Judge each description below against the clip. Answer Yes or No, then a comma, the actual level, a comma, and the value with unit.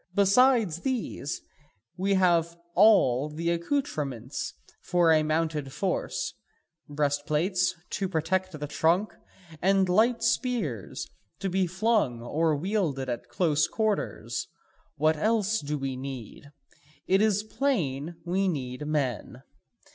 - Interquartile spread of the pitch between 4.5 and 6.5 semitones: Yes, average, 5.3 semitones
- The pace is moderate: No, slow, 115 wpm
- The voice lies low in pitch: No, medium, 170 Hz